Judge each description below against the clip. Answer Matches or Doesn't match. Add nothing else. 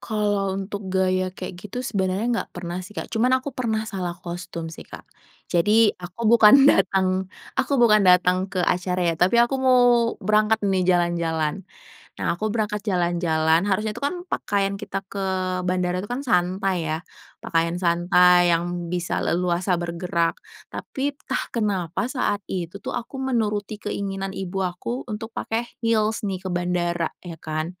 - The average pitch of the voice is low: Doesn't match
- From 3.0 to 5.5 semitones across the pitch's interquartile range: Matches